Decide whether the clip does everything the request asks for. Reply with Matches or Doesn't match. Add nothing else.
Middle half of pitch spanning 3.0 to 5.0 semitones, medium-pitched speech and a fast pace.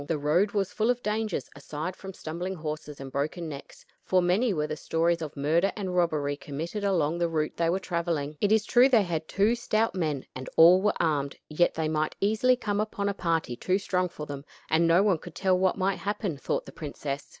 Matches